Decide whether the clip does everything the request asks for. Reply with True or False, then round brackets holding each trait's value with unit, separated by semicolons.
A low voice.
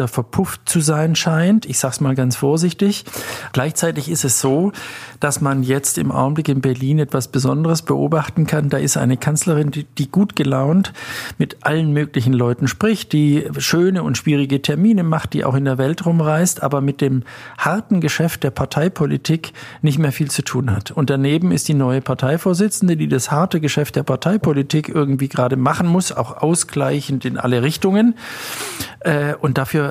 False (150 Hz)